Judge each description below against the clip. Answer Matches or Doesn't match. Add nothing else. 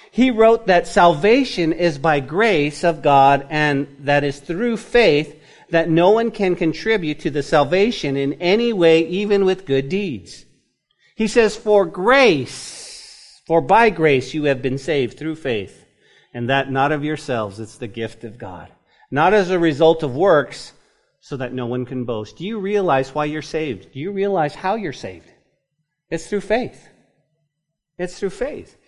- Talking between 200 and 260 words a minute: Doesn't match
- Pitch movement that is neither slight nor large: Doesn't match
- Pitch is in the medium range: Matches